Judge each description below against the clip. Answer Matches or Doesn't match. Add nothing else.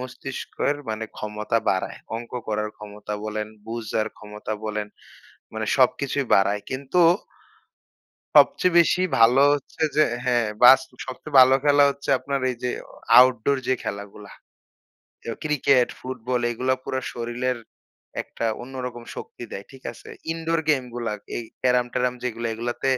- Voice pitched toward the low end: Matches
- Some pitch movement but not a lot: Matches